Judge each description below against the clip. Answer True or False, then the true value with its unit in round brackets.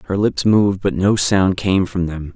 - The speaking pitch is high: False (95 Hz)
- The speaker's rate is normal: False (230 wpm)